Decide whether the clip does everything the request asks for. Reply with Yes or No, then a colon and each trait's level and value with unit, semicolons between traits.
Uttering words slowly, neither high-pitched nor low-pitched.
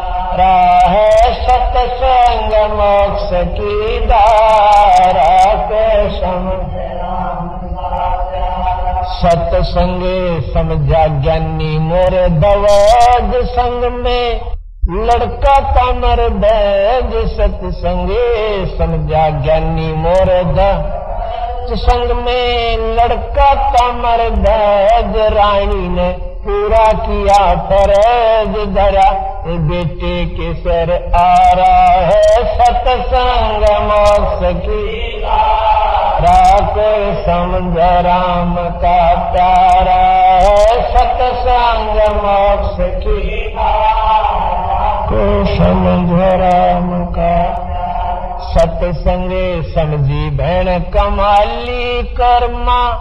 No: slow, 70 wpm; high, 205 Hz